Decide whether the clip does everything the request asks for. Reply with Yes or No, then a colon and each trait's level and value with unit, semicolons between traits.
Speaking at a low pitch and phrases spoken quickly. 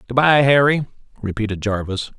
No: low, 120 Hz; slow, 135 wpm